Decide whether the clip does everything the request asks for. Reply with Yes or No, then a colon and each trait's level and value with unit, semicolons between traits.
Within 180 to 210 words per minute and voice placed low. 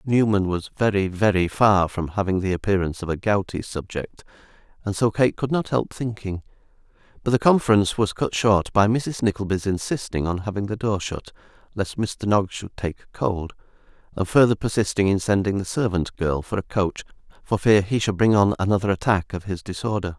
Yes: average, 185 wpm; low, 100 Hz